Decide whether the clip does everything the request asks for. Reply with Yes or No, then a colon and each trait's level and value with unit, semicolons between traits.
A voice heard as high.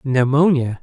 No: low, 135 Hz